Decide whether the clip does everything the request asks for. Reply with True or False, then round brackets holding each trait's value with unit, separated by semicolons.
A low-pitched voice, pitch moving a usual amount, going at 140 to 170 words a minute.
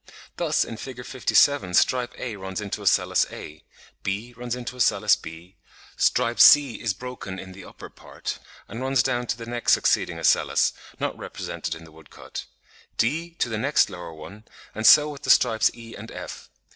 False (115 Hz; 4.6 semitones; 180 wpm)